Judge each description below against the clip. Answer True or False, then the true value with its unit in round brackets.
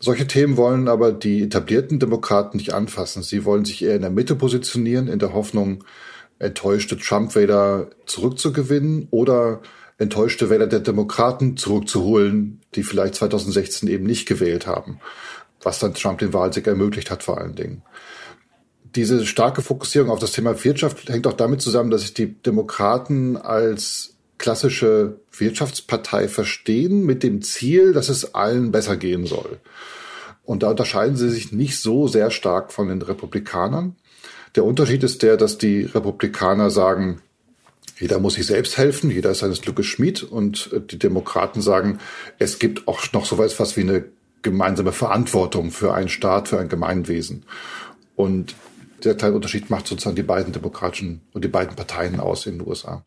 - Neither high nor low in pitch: False (110 Hz)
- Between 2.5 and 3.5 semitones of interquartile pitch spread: False (4.0 semitones)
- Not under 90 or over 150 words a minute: False (160 wpm)